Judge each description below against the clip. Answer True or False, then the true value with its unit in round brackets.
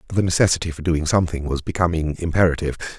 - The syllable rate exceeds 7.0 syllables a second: True (7.3 syllables/s)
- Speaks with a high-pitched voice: False (80 Hz)